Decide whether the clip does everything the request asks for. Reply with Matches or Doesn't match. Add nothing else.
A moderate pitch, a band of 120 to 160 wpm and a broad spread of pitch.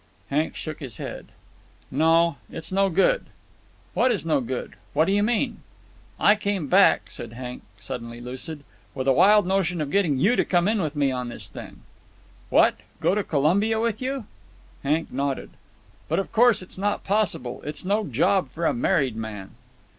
Doesn't match